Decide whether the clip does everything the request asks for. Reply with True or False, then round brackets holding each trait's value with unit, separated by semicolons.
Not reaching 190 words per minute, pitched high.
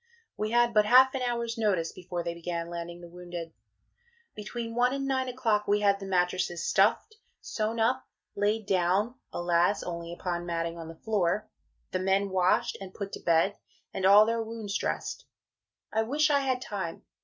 True (180 wpm; 200 Hz)